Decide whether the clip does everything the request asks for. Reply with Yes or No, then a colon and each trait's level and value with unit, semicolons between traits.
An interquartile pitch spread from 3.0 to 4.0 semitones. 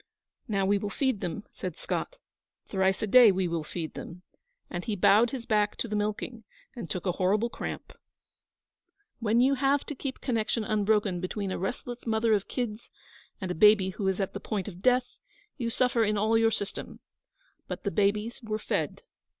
Yes: average, 3.3 semitones